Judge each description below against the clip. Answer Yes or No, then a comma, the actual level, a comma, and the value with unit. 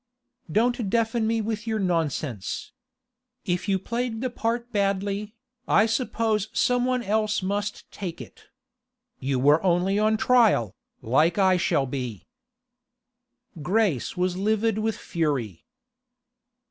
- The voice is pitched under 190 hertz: No, high, 205 Hz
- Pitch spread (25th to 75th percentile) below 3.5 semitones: No, average, 4.6 semitones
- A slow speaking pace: Yes, slow, 120 wpm